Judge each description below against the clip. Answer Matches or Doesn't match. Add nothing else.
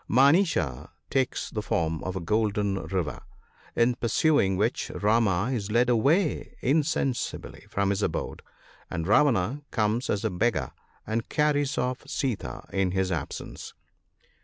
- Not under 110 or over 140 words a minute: Matches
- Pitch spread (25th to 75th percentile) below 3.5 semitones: Doesn't match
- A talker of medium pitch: Doesn't match